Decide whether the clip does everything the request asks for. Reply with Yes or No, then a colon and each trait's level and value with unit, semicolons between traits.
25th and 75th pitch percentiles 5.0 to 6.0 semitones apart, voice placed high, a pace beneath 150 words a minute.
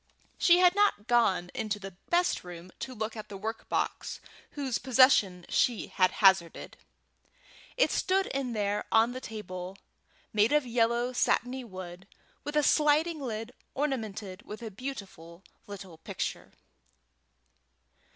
Yes: wide, 5.4 semitones; high, 225 Hz; slow, 135 wpm